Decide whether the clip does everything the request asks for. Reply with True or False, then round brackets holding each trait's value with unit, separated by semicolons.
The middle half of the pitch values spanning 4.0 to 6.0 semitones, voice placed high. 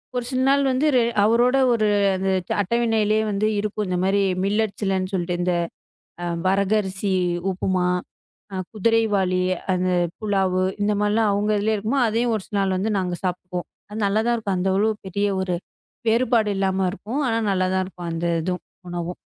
False (3.0 semitones; 200 Hz)